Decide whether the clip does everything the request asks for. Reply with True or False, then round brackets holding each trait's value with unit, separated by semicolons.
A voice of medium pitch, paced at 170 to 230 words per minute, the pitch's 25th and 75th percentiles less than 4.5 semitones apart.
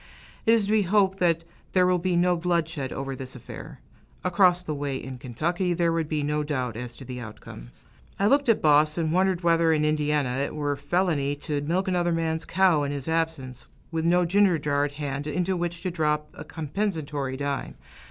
True (160 Hz; 200 wpm; 3.8 semitones)